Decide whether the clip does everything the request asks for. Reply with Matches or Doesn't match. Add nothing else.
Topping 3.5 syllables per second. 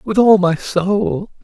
Doesn't match